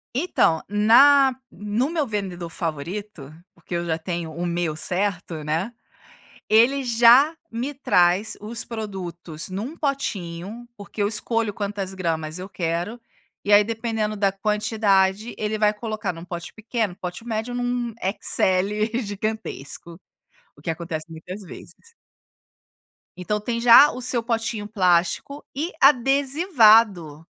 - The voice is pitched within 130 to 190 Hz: No, high, 210 Hz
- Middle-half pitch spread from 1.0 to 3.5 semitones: No, average, 4.8 semitones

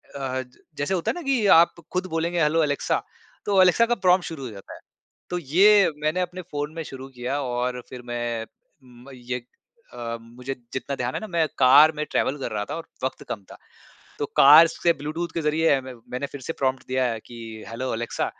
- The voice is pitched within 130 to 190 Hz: Yes, medium, 140 Hz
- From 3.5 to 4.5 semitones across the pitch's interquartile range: No, average, 5.1 semitones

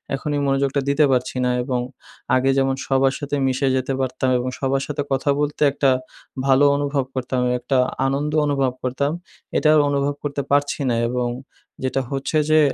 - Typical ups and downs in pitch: No, narrow, 1.5 semitones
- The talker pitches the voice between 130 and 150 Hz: Yes, low, 135 Hz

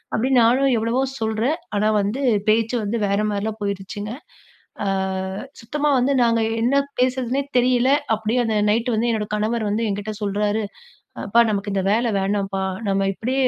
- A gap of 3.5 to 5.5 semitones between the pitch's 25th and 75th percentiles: No, average, 3.0 semitones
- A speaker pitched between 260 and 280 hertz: No, high, 220 Hz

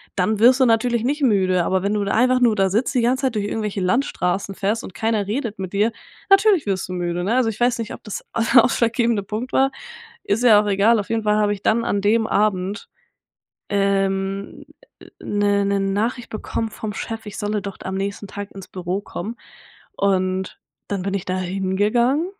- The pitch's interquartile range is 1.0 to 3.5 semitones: Yes, average, 2.9 semitones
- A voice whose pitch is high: Yes, high, 205 Hz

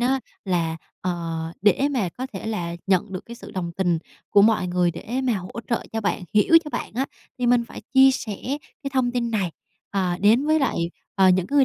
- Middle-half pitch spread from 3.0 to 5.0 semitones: No, wide, 5.6 semitones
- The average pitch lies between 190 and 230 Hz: Yes, high, 210 Hz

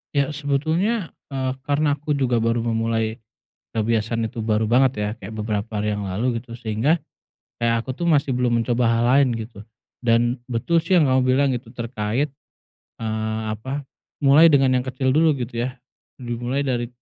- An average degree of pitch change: Yes, average, 3.5 semitones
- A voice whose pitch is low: Yes, low, 120 Hz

